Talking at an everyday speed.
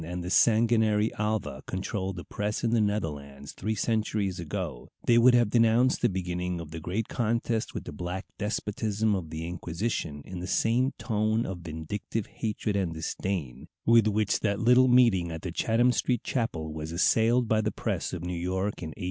Yes: average, 185 wpm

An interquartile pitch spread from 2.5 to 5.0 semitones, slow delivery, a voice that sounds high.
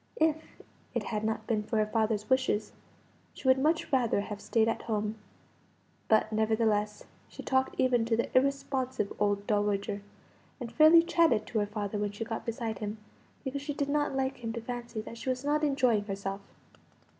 No: average, 3.9 semitones; average, 180 wpm; high, 225 Hz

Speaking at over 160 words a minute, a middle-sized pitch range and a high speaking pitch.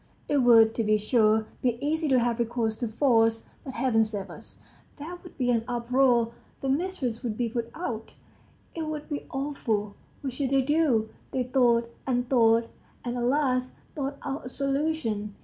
Yes: average, 180 wpm; average, 3.4 semitones; high, 245 Hz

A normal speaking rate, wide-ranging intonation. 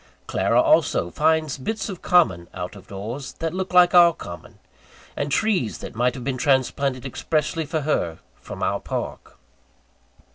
Yes: average, 155 wpm; wide, 5.9 semitones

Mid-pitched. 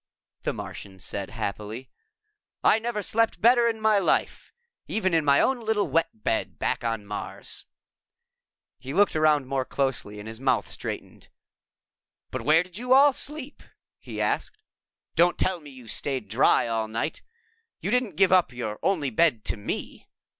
Yes: medium, 155 Hz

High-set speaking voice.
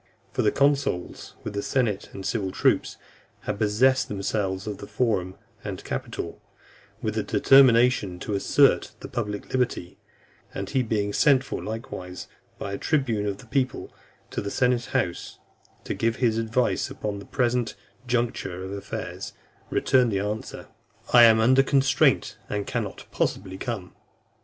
No: low, 110 Hz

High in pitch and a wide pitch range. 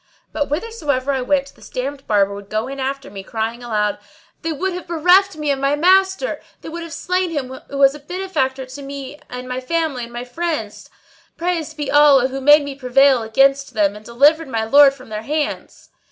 No: very high, 275 Hz; average, 3.9 semitones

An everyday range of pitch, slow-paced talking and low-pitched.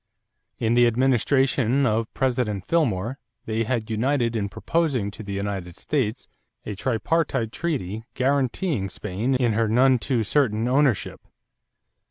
Yes: average, 3.7 semitones; slow, 130 wpm; low, 120 Hz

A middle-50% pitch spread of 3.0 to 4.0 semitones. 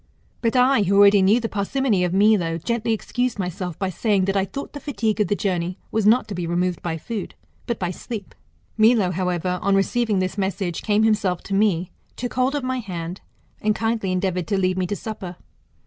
Yes: average, 3.5 semitones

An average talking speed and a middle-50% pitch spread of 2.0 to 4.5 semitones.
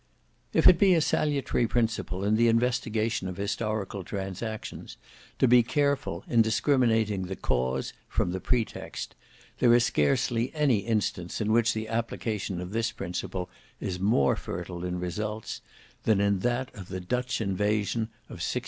Yes: average, 155 wpm; average, 4.0 semitones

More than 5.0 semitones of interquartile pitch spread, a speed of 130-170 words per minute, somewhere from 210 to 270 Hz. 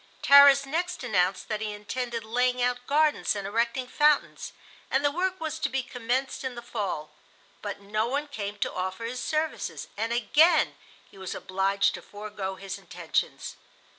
Yes: wide, 5.4 semitones; average, 165 wpm; high, 240 Hz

